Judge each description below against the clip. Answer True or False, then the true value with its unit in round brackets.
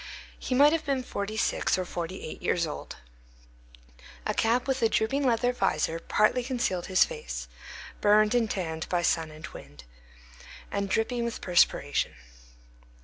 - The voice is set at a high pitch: True (215 Hz)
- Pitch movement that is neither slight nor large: False (5.8 semitones)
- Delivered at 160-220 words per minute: False (150 wpm)